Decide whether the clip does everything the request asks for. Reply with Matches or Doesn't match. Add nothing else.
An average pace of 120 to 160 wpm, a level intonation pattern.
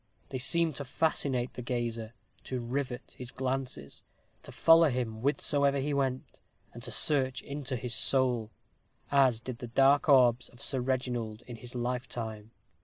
Matches